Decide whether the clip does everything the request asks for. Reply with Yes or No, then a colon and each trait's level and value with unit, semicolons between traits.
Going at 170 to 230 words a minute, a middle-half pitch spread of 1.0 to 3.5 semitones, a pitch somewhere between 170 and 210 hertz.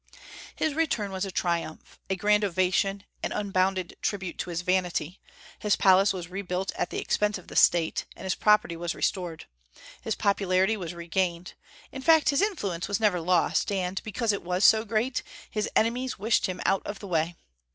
Yes: average, 185 wpm; average, 2.8 semitones; high, 190 Hz